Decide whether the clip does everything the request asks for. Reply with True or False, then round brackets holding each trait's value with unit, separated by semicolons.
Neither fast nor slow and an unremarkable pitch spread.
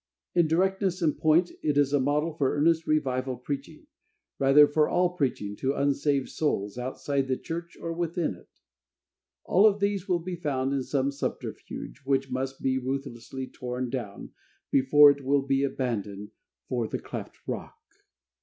True (160 wpm; 3.6 semitones)